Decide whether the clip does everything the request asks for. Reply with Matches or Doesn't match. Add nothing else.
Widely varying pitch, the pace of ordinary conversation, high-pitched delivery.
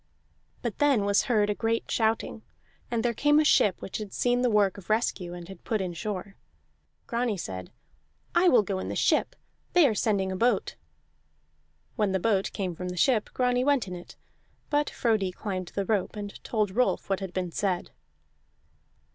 Doesn't match